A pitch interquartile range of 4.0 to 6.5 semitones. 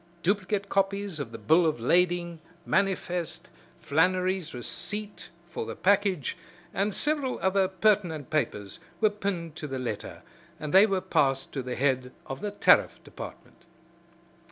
Yes: wide, 5.4 semitones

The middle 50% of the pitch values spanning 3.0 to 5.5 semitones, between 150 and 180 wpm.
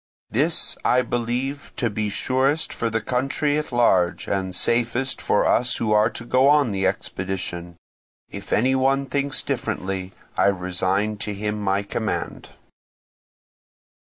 No: average, 5.2 semitones; average, 140 wpm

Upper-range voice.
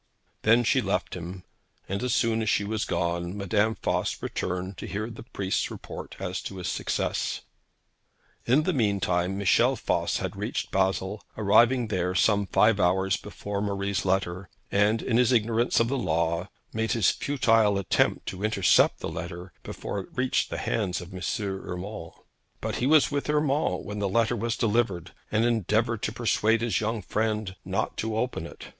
No: low, 105 Hz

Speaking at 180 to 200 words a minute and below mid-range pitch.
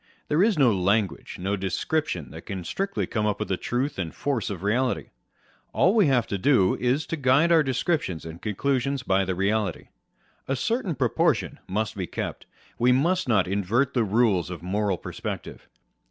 Yes: average, 185 wpm; low, 115 Hz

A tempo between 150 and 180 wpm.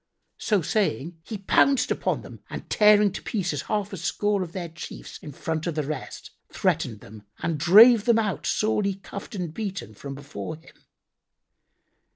Yes: average, 170 wpm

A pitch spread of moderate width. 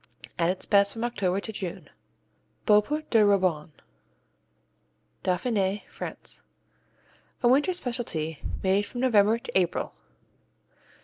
Yes: average, 4.3 semitones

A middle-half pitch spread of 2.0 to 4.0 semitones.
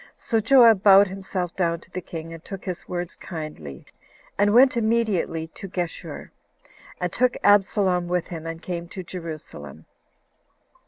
Yes: average, 3.5 semitones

